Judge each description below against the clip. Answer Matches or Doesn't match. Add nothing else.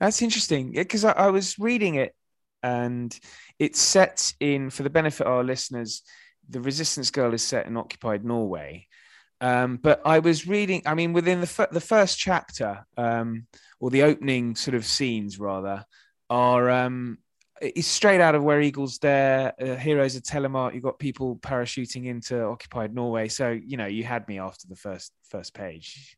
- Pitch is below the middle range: Matches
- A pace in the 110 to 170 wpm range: Doesn't match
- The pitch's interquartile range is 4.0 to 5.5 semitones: Matches